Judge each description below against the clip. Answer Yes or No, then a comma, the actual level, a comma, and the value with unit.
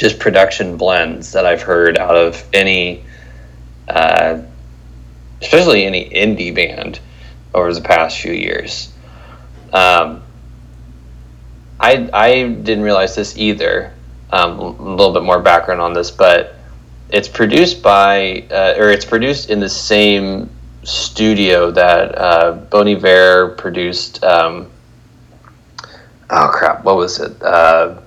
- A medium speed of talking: No, slow, 120 wpm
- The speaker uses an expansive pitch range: Yes, wide, 8.3 semitones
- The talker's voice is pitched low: Yes, very low, 85 Hz